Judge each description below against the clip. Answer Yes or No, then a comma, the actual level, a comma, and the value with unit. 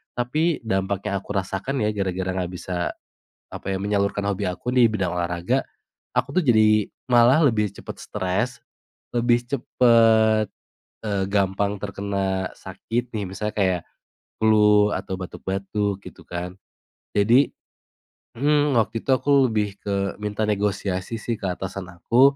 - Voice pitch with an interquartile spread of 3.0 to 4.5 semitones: Yes, average, 3.3 semitones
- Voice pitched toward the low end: Yes, low, 105 Hz